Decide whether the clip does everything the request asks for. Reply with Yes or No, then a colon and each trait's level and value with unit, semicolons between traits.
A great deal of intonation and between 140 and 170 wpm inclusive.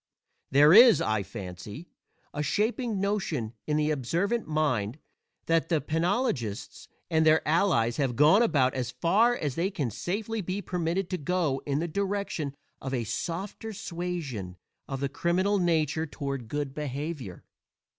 Yes: wide, 5.8 semitones; average, 145 wpm